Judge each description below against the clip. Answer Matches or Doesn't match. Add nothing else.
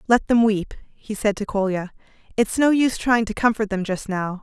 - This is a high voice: Matches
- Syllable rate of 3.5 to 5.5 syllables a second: Matches